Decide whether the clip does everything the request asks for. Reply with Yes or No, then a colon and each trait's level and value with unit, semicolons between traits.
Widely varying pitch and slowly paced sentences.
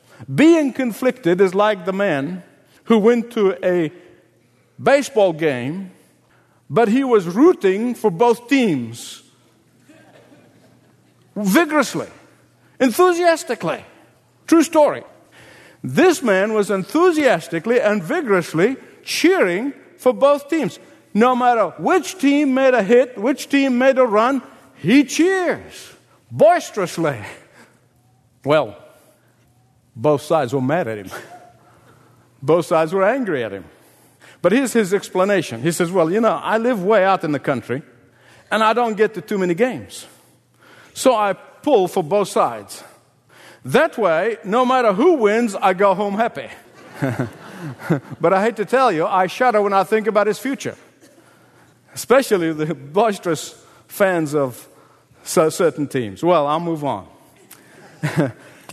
Yes: wide, 7.9 semitones; slow, 130 wpm